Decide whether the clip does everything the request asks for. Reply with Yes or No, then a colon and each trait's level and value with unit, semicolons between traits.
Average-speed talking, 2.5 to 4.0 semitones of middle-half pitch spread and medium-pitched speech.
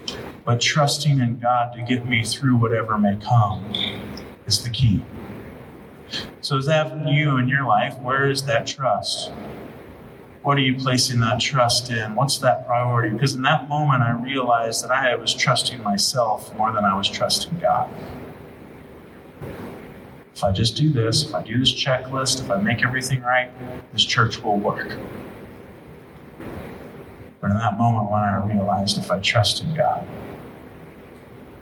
No: average, 160 wpm; average, 3.3 semitones; low, 125 Hz